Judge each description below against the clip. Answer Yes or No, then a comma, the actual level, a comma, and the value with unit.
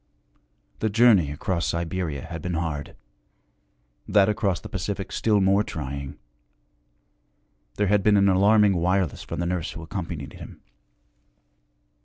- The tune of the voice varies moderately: Yes, average, 3.6 semitones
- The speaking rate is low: Yes, slow, 130 wpm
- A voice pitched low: Yes, very low, 95 Hz